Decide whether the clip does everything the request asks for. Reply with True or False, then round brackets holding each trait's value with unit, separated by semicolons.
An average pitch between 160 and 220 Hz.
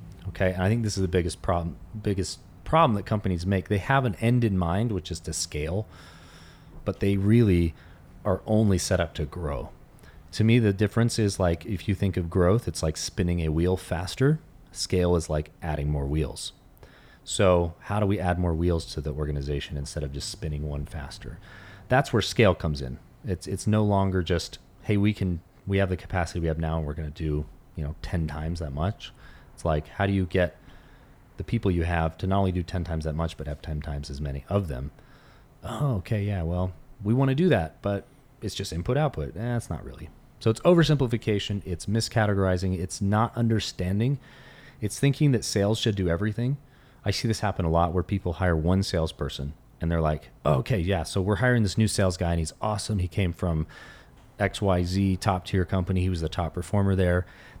False (95 Hz)